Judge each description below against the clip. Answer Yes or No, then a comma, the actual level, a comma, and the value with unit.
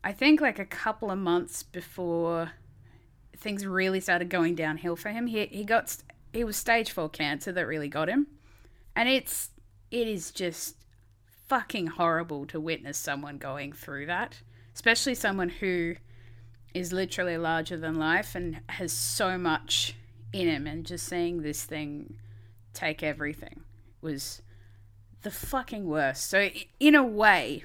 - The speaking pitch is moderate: Yes, medium, 160 Hz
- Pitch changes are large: Yes, wide, 8.4 semitones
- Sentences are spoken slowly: No, average, 150 wpm